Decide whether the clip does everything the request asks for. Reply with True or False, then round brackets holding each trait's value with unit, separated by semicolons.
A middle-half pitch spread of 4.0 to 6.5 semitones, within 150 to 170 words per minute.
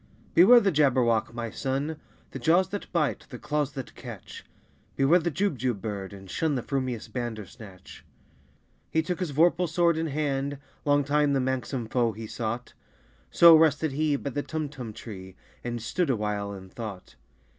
True (5.2 semitones; 165 wpm)